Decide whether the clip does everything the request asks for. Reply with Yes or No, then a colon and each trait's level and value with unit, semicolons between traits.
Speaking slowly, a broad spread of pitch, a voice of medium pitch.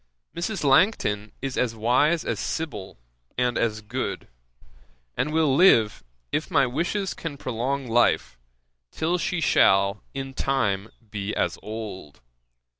No: slow, 125 wpm; wide, 6.7 semitones; low, 130 Hz